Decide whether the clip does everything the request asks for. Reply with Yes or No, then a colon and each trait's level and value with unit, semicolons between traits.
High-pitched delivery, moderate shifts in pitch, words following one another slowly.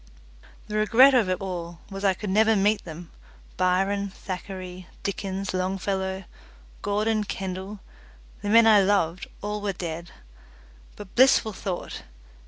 No: high, 195 Hz; narrow, 2.2 semitones; slow, 130 wpm